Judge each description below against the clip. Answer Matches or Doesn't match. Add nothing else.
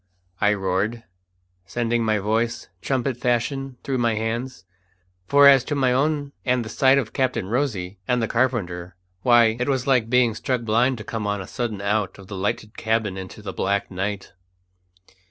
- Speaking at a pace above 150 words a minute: Matches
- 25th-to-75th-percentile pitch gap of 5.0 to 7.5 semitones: Doesn't match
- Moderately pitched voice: Doesn't match